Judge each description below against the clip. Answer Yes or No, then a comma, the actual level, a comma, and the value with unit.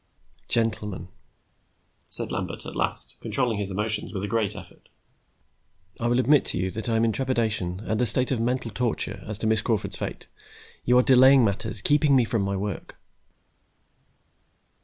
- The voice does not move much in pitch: No, average, 3.0 semitones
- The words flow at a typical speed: Yes, average, 170 wpm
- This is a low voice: Yes, low, 115 Hz